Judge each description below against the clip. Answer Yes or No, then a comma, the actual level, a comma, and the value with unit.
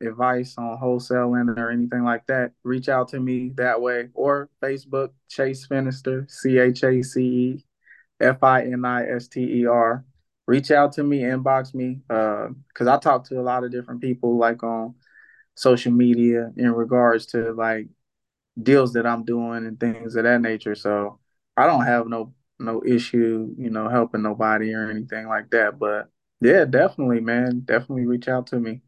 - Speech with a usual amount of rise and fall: No, narrow, 1.8 semitones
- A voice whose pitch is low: Yes, low, 120 Hz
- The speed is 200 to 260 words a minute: No, average, 160 wpm